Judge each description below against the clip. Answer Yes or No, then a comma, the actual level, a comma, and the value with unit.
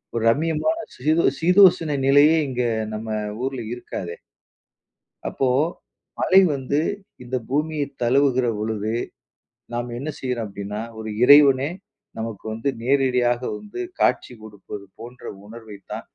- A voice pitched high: No, low, 125 Hz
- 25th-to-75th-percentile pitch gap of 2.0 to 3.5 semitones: No, average, 4.2 semitones